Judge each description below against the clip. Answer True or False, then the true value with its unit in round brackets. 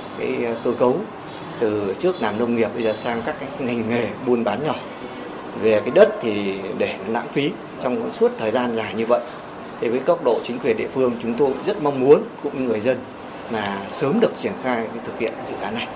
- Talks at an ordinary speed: True (220 wpm)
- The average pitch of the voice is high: False (115 Hz)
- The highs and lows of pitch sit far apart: False (2.3 semitones)